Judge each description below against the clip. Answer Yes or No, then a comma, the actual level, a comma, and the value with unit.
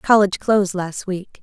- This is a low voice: No, high, 190 Hz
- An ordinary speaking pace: Yes, average, 170 wpm